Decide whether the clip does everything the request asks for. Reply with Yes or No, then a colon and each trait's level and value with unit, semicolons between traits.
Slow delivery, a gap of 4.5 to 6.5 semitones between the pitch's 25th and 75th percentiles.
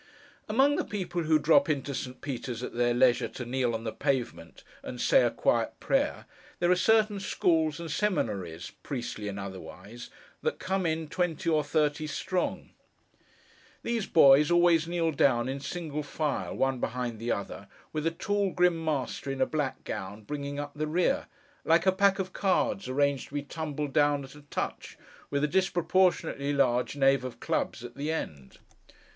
No: average, 175 wpm; average, 5.1 semitones